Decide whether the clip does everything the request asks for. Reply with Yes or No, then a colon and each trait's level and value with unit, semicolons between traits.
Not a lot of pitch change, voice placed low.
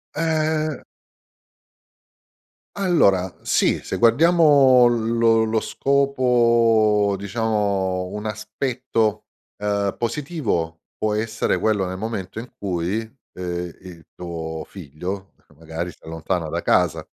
No: average, 4.6 semitones; low, 105 Hz